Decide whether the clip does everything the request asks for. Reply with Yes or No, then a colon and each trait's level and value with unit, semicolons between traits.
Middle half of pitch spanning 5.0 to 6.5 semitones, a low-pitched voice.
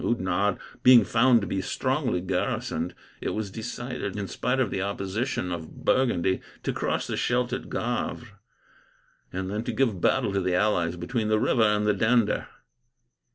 No: average, 4.2 semitones; low, 105 Hz